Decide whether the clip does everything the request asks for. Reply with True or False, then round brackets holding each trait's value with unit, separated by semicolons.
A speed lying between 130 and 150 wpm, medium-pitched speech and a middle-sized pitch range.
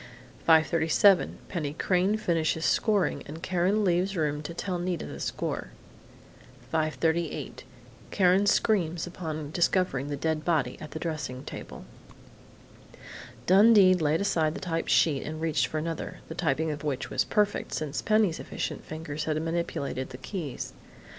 True (140 wpm; 165 Hz; 3.0 semitones)